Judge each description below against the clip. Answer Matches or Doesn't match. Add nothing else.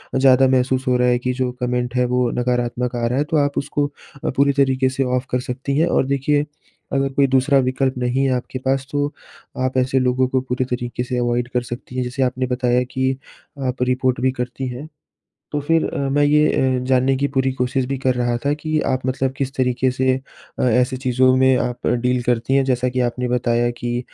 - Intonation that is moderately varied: Doesn't match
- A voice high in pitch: Doesn't match